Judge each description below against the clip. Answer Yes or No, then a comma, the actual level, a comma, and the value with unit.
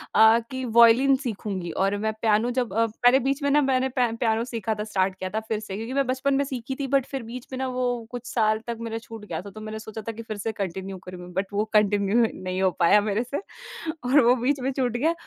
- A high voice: Yes, high, 225 Hz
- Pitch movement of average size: Yes, average, 3.6 semitones